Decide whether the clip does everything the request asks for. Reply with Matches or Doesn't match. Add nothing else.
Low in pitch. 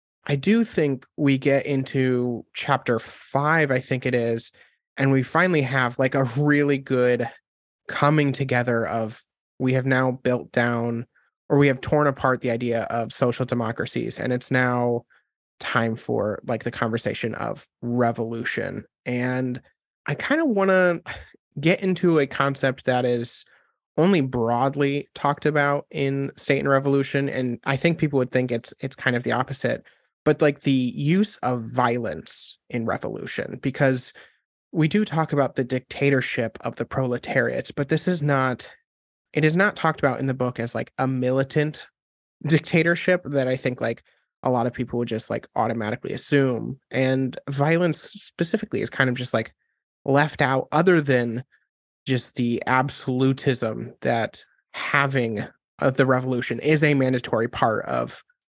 Matches